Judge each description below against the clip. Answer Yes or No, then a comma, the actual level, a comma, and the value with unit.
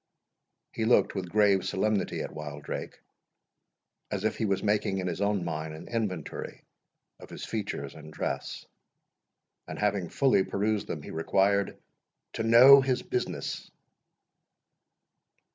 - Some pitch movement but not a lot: Yes, average, 4.2 semitones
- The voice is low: Yes, low, 100 Hz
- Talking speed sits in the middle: No, slow, 130 wpm